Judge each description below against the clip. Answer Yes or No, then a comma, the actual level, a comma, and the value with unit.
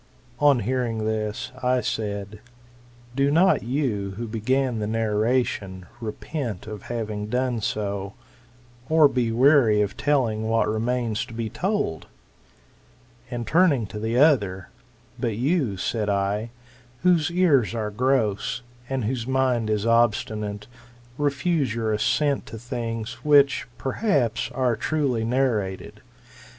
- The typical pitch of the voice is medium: No, low, 115 Hz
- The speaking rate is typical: No, slow, 125 wpm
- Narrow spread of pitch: No, average, 3.8 semitones